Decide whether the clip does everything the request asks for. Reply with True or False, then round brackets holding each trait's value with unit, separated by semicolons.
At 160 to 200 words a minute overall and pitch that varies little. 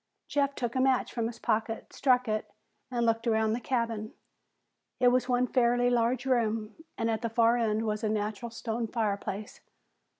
True (175 wpm; 2.0 semitones)